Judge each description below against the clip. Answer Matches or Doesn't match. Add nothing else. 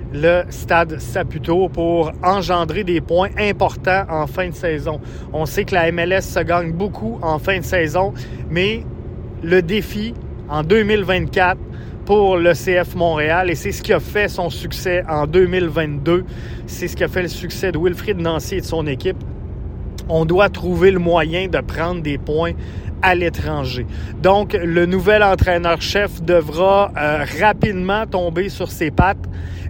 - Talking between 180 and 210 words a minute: Doesn't match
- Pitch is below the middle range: Doesn't match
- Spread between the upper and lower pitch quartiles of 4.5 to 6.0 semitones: Doesn't match